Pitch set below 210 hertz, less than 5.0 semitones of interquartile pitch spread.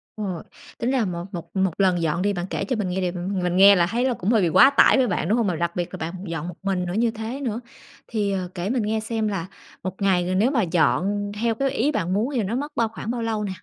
Yes: high, 200 Hz; average, 4.3 semitones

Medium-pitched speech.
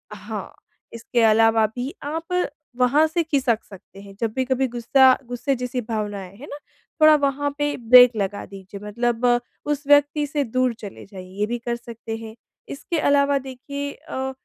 No: very high, 250 Hz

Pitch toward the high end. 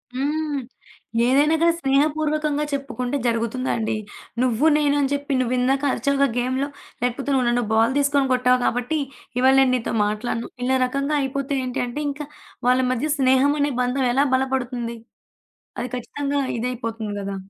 Yes: very high, 265 Hz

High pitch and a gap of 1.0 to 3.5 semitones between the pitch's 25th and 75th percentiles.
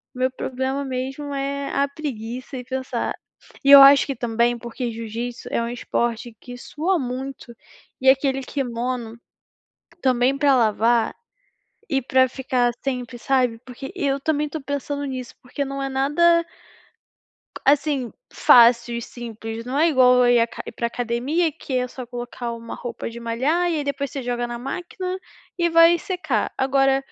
Yes: very high, 260 Hz; average, 2.7 semitones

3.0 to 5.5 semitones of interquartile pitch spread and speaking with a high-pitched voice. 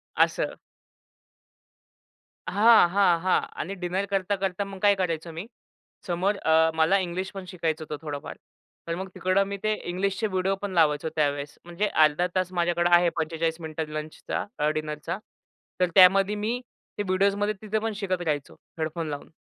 No: average, 3.5 semitones; medium, 180 Hz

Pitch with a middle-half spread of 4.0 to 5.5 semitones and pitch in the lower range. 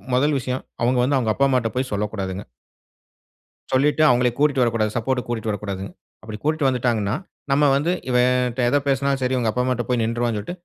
No: average, 3.1 semitones; low, 125 Hz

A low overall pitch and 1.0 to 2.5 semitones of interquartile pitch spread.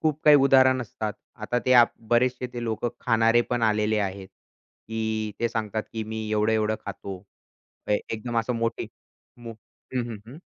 Yes: low, 115 Hz; narrow, 2.1 semitones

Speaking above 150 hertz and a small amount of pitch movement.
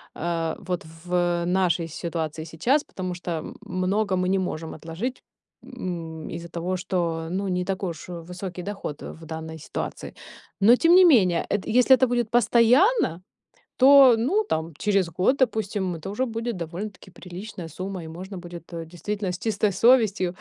No: medium, 185 Hz; average, 4.4 semitones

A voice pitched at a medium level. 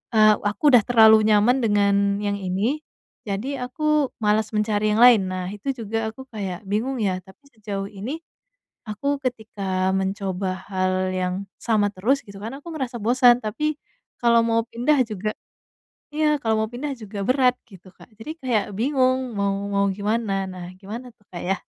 No: high, 215 Hz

